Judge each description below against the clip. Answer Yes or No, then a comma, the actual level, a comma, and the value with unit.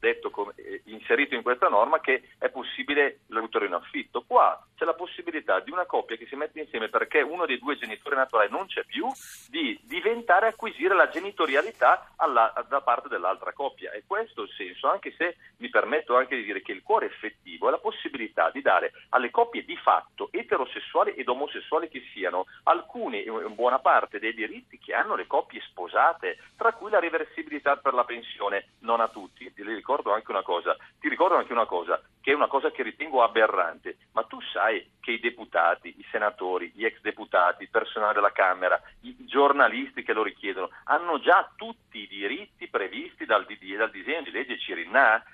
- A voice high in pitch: Yes, high, 235 Hz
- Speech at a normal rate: No, fast, 185 wpm